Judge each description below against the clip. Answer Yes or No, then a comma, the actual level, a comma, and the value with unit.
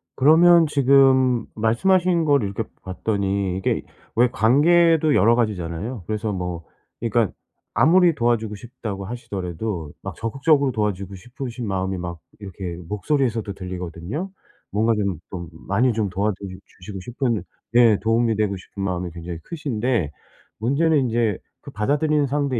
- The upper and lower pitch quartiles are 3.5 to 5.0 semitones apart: No, wide, 5.5 semitones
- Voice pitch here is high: No, low, 110 Hz